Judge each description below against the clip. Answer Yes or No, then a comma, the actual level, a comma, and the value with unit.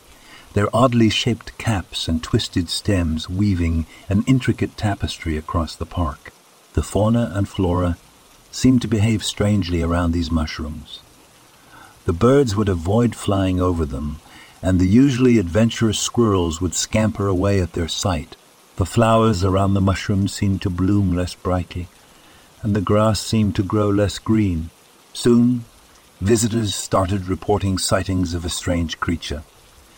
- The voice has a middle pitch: No, low, 100 Hz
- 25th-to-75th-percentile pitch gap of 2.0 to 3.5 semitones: No, average, 4.0 semitones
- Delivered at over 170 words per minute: No, average, 140 wpm